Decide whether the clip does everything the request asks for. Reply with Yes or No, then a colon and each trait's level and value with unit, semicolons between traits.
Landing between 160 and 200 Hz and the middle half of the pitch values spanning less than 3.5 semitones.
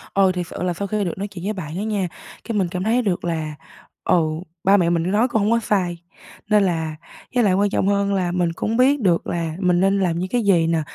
Yes: high, 190 Hz; average, 3.0 semitones